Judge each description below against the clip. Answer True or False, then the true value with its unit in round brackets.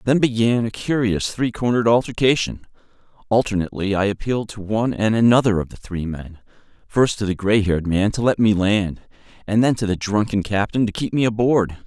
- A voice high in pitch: False (110 Hz)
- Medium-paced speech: True (185 wpm)